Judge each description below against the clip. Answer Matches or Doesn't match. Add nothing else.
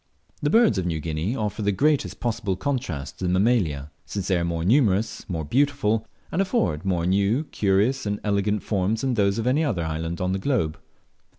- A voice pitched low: Matches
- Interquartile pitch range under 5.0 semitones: Doesn't match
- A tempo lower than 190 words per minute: Doesn't match